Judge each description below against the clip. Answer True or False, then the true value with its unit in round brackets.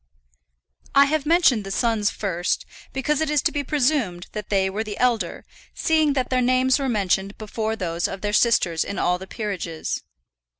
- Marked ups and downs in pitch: True (5.7 semitones)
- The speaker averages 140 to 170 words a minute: False (180 wpm)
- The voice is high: True (220 Hz)